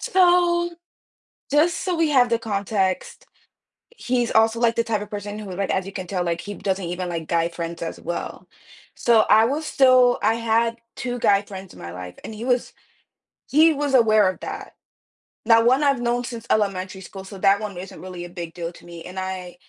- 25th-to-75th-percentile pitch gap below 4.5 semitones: No, average, 4.8 semitones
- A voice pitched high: Yes, high, 210 Hz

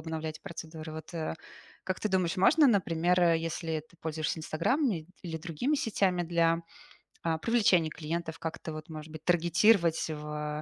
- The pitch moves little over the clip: Yes, narrow, 2.2 semitones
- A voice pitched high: No, medium, 165 Hz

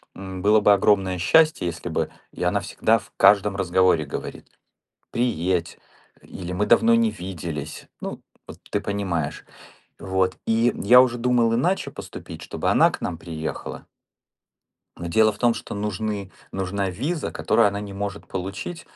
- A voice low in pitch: Yes, low, 100 Hz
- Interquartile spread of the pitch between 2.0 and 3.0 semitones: No, average, 3.7 semitones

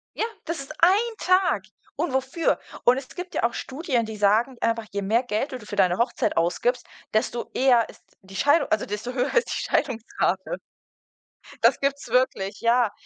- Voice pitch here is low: No, high, 245 Hz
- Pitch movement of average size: Yes, average, 4.3 semitones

